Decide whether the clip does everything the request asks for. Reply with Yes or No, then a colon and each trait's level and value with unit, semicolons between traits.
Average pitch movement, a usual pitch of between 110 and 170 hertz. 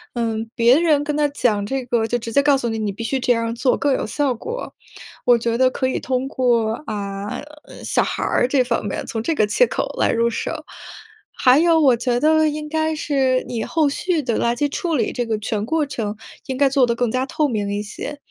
No: average, 4.1 semitones; very high, 250 Hz